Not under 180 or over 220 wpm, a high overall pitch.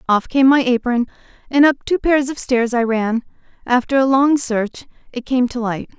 Yes: average, 200 wpm; very high, 250 Hz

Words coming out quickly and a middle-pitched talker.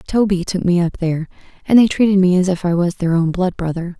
Yes: fast, 255 wpm; medium, 180 Hz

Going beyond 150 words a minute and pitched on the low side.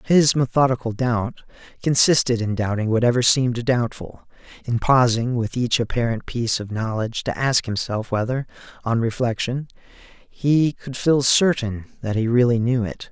No: average, 145 wpm; low, 120 Hz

